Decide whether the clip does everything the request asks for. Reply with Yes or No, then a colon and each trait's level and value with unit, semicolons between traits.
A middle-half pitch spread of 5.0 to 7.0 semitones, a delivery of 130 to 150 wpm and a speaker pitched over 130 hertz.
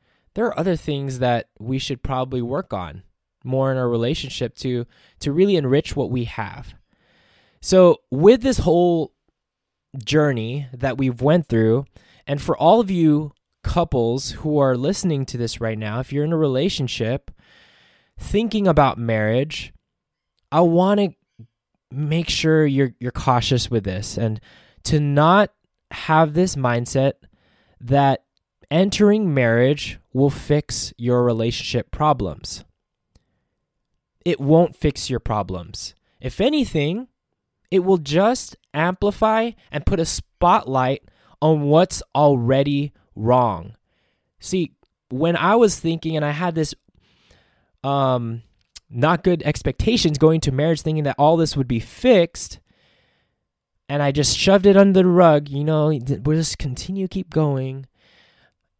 Yes: average, 5.3 semitones; slow, 135 wpm; medium, 140 Hz